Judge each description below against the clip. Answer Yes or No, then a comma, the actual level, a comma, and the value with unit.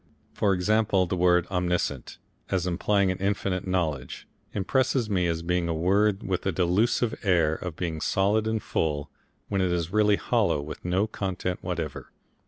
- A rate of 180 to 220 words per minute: No, average, 160 wpm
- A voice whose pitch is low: Yes, very low, 90 Hz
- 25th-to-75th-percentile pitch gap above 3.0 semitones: No, average, 2.7 semitones